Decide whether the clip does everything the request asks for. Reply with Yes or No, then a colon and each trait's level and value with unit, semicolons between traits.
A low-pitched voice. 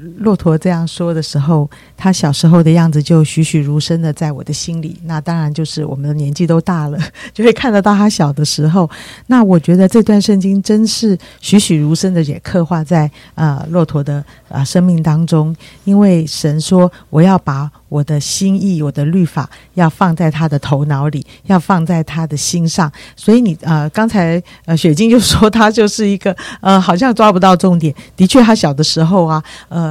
No: medium, 165 Hz